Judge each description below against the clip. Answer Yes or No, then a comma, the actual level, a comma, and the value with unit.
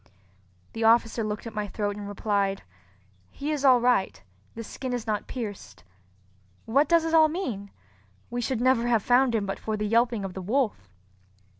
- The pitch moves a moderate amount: Yes, average, 3.5 semitones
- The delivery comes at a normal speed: Yes, average, 180 wpm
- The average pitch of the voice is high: Yes, high, 225 Hz